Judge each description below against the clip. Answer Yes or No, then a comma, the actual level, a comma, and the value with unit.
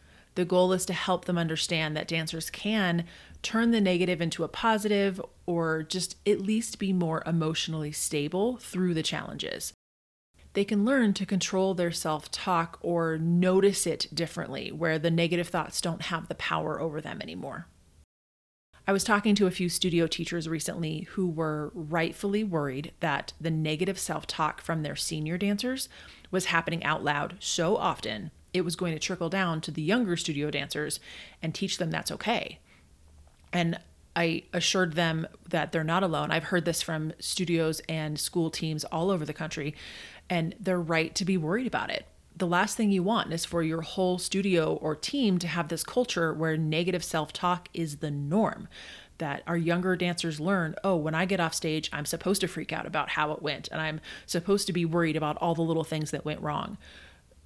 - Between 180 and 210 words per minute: Yes, average, 185 wpm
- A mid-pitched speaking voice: Yes, medium, 170 Hz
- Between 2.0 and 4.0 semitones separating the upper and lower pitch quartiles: Yes, average, 2.8 semitones